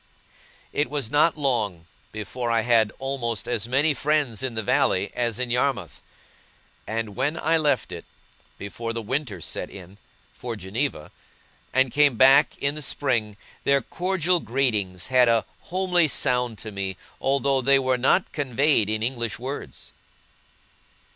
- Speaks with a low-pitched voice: Yes, low, 125 Hz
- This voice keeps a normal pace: Yes, average, 145 wpm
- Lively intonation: No, average, 4.0 semitones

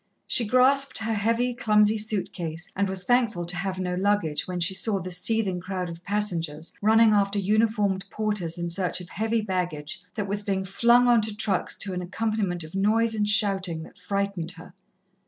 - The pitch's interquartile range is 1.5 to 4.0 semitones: Yes, average, 3.3 semitones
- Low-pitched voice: No, high, 200 Hz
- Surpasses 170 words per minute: Yes, average, 190 wpm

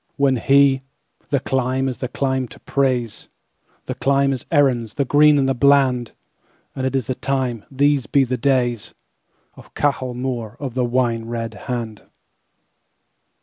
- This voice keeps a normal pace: No, slow, 125 wpm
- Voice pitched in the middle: No, low, 130 Hz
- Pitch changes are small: Yes, narrow, 2.2 semitones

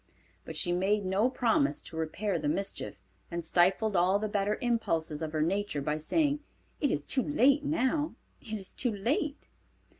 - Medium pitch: No, high, 205 Hz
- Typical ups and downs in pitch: No, wide, 6.8 semitones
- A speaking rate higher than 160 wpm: Yes, average, 175 wpm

